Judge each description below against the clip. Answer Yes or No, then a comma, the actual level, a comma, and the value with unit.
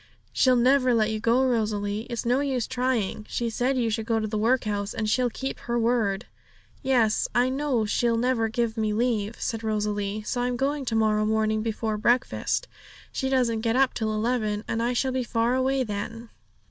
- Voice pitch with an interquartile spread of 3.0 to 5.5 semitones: No, narrow, 2.6 semitones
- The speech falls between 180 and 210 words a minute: Yes, average, 195 wpm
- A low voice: No, high, 230 Hz